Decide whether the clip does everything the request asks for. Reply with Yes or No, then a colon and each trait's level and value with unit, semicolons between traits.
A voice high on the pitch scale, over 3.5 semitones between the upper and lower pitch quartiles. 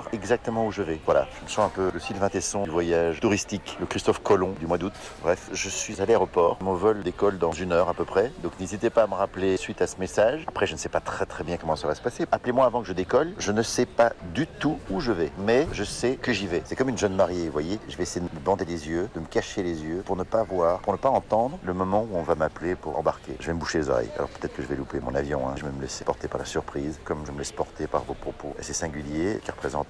No: very low, 90 Hz; average, 3.9 semitones